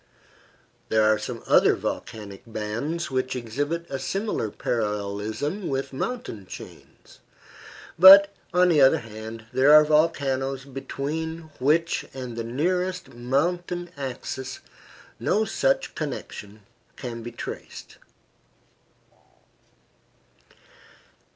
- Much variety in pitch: Yes, wide, 6.5 semitones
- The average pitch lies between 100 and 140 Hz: Yes, low, 135 Hz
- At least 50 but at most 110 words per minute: Yes, slow, 100 wpm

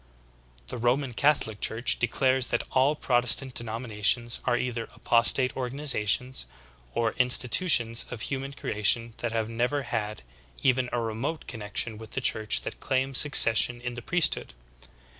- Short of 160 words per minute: Yes, average, 140 wpm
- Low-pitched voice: Yes, low, 120 Hz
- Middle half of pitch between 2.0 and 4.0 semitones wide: Yes, narrow, 2.5 semitones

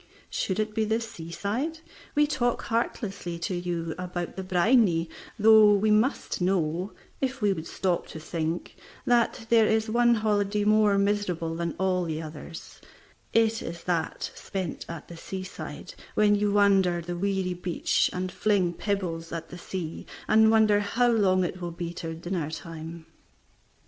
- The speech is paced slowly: No, average, 160 wpm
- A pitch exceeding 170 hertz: Yes, high, 190 Hz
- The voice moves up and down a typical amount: Yes, average, 4.0 semitones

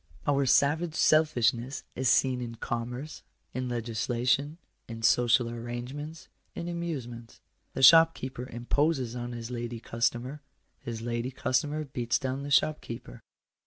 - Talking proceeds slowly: Yes, slow, 125 wpm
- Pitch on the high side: No, low, 125 Hz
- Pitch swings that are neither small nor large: Yes, average, 3.3 semitones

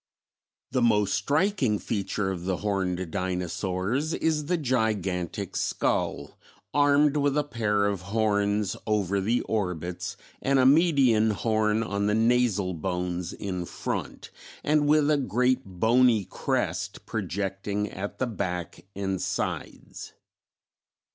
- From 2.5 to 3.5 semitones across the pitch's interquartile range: No, average, 5.1 semitones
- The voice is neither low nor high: No, low, 105 Hz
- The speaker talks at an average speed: No, slow, 120 wpm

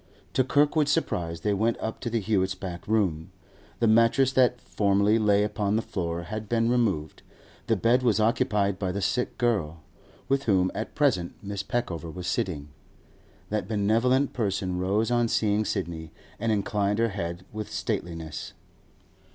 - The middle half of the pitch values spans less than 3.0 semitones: No, average, 3.9 semitones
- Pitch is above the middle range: No, low, 105 Hz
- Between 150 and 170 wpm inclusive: Yes, average, 160 wpm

